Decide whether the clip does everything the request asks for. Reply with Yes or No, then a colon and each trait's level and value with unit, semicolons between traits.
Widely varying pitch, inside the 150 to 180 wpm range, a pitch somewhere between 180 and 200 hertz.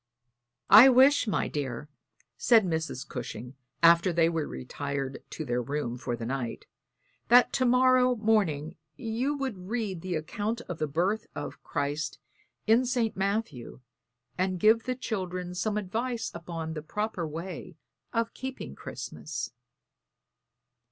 No: wide, 6.8 semitones; slow, 135 wpm; medium, 185 Hz